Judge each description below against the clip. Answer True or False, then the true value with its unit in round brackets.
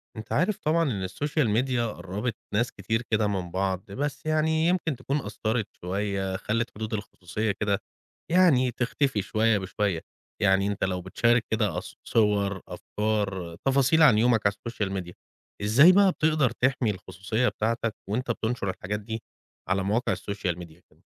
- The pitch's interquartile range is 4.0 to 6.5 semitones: True (4.3 semitones)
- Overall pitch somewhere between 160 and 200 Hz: False (110 Hz)